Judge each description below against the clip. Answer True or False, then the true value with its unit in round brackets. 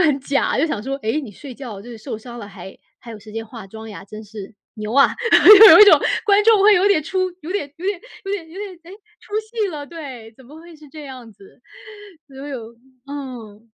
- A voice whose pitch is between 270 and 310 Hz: True (275 Hz)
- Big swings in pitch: True (7.4 semitones)